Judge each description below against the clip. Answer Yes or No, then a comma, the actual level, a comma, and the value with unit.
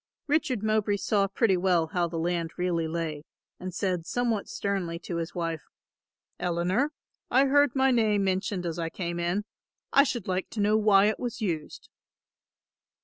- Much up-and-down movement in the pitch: No, average, 4.0 semitones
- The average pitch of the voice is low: No, high, 190 Hz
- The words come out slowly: No, average, 165 wpm